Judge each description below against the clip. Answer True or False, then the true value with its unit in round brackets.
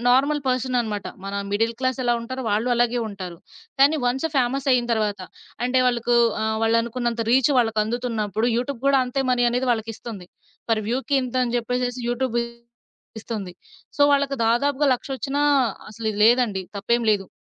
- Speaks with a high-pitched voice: True (240 Hz)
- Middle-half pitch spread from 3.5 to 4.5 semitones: False (2.6 semitones)